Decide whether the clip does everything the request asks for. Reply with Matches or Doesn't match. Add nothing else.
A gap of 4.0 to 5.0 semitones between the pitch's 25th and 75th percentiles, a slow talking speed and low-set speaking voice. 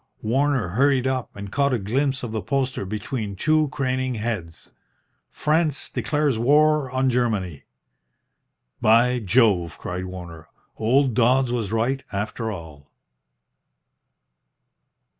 Matches